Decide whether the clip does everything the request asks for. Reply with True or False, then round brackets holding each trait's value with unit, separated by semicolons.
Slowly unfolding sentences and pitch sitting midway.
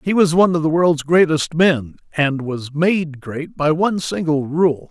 False (195 wpm; 160 Hz)